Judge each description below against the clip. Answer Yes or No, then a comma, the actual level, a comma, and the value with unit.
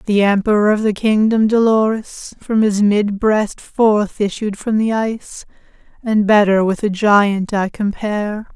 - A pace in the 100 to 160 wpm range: Yes, average, 155 wpm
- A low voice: No, high, 210 Hz